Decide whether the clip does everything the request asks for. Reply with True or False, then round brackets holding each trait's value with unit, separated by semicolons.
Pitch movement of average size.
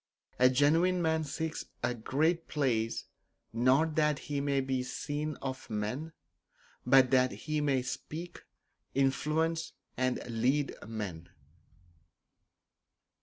True (3.4 semitones)